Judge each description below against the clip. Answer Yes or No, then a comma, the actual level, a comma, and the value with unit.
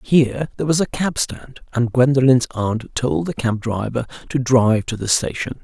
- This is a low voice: Yes, low, 125 Hz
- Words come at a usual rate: Yes, average, 190 wpm